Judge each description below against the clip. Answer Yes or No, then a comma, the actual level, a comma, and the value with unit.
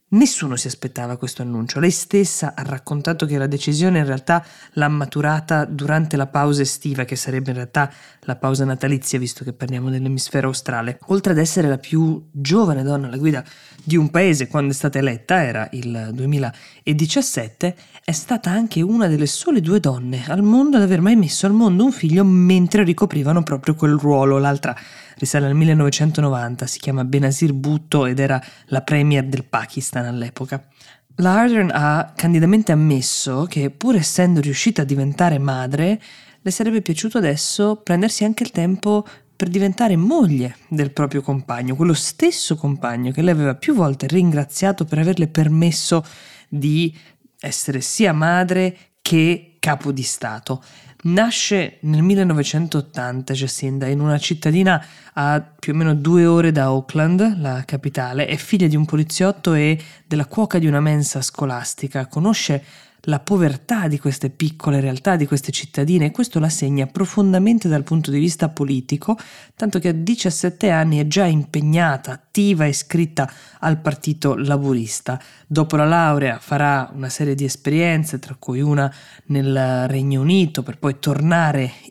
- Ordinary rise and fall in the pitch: Yes, average, 3.9 semitones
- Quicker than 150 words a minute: Yes, average, 160 wpm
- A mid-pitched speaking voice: Yes, medium, 150 Hz